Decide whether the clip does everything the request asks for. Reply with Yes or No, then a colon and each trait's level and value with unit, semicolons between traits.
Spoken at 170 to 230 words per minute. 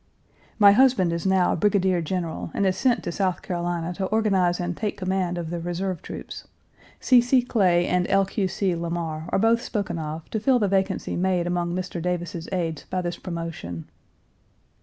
Yes: average, 180 wpm